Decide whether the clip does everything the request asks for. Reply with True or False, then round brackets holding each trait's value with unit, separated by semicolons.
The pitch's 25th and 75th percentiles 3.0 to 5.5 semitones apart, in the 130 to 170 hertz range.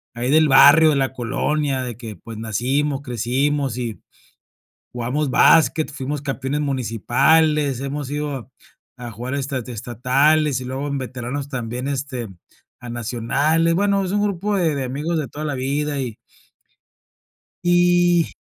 True (3.3 semitones; 140 Hz)